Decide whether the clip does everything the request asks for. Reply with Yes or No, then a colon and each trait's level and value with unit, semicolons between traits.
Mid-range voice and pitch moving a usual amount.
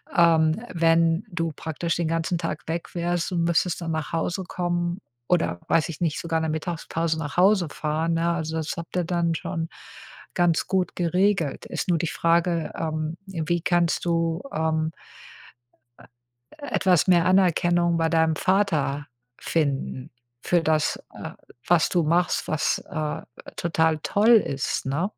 No: medium, 165 Hz; narrow, 1.6 semitones